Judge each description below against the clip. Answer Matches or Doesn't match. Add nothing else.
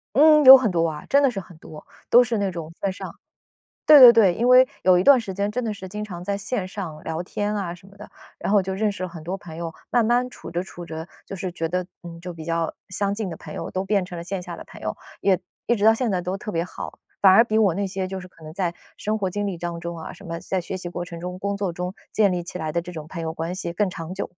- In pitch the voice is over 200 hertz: Doesn't match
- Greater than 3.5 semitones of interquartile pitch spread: Doesn't match